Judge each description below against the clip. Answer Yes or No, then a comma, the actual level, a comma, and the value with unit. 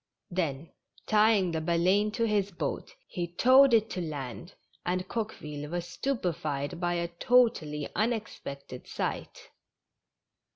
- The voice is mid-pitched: Yes, medium, 175 Hz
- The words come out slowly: Yes, slow, 125 wpm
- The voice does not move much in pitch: No, wide, 5.5 semitones